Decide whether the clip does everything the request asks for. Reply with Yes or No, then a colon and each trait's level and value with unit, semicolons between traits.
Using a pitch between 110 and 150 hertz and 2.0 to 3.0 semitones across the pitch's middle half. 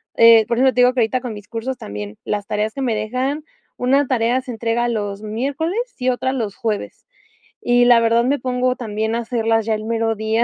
No: high, 230 Hz; narrow, 2.5 semitones